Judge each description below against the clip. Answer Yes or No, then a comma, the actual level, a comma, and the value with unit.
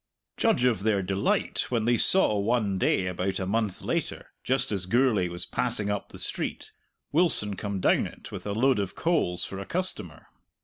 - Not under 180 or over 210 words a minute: Yes, average, 185 wpm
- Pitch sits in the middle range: No, low, 105 Hz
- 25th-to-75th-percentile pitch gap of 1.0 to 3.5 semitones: No, average, 4.2 semitones